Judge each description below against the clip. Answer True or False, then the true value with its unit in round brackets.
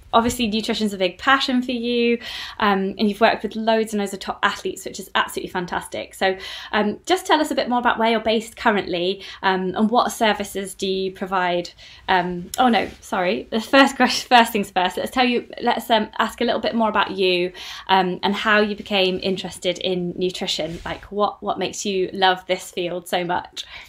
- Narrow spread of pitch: False (3.7 semitones)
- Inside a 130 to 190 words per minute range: False (205 wpm)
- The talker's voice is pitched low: False (205 Hz)